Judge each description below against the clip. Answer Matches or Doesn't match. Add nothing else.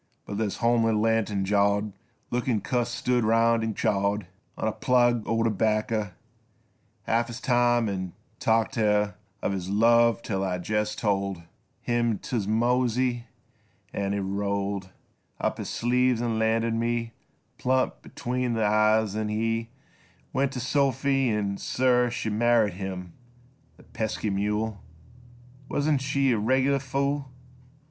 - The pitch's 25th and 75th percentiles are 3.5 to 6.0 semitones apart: Doesn't match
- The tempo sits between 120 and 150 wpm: Matches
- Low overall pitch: Matches